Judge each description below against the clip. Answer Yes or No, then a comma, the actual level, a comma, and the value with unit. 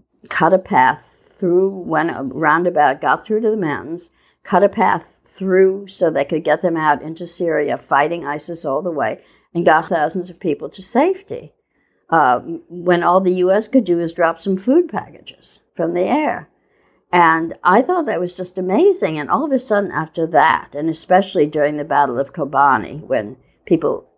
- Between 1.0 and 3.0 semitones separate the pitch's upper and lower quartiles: No, average, 3.4 semitones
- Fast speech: No, average, 185 wpm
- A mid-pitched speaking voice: Yes, medium, 175 Hz